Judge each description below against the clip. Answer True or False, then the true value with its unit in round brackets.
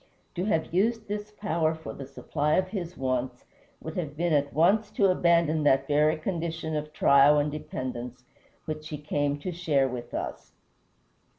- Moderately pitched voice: True (155 Hz)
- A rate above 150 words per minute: True (170 wpm)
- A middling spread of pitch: True (3.3 semitones)